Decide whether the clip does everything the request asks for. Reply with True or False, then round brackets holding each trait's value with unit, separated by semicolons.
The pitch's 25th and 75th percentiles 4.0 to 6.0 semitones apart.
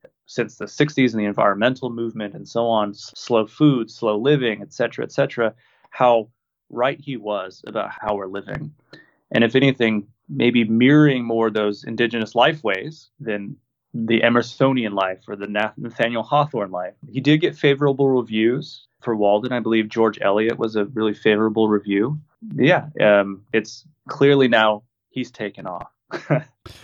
False (3.4 semitones)